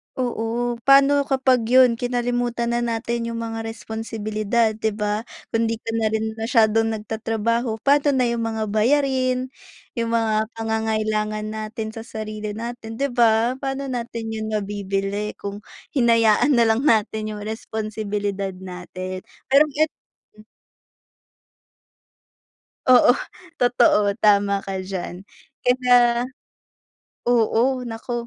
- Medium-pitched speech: No, high, 225 Hz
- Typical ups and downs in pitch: No, narrow, 2.0 semitones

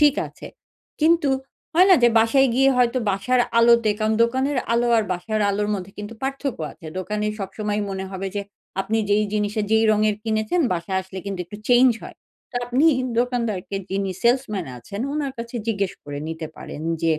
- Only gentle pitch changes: No, average, 4.0 semitones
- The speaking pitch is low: No, high, 215 Hz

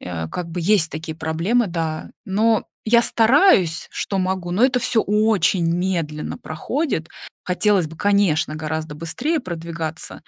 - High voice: No, medium, 175 Hz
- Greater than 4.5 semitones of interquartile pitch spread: Yes, average, 4.9 semitones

